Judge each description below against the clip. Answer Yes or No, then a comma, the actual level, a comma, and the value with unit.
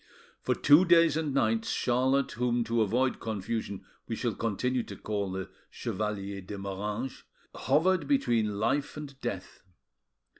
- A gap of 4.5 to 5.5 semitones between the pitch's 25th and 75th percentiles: Yes, average, 4.9 semitones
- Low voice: Yes, low, 115 Hz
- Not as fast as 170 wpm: Yes, average, 140 wpm